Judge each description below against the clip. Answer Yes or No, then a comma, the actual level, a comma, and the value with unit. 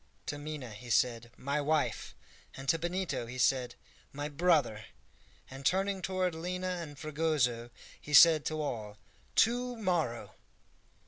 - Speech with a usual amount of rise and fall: No, wide, 5.9 semitones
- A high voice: No, medium, 150 Hz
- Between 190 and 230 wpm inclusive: No, slow, 135 wpm